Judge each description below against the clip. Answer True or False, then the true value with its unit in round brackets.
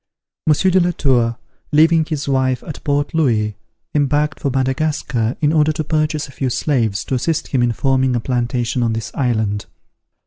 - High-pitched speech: False (135 Hz)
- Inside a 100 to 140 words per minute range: False (175 wpm)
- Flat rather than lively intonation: False (4.0 semitones)